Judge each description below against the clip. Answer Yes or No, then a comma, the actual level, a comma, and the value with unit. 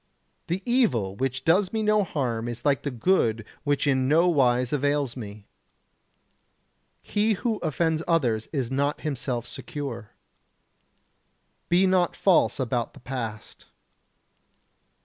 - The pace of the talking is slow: Yes, slow, 125 wpm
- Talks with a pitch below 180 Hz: Yes, medium, 140 Hz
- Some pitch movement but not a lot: No, wide, 6.1 semitones